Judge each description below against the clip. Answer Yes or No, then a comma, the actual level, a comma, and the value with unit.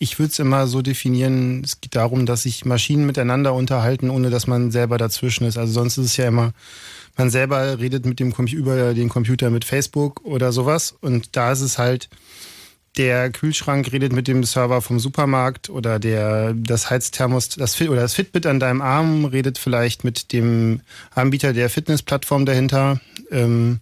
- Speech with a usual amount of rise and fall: No, narrow, 1.9 semitones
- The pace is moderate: Yes, average, 180 wpm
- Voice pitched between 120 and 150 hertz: Yes, low, 125 Hz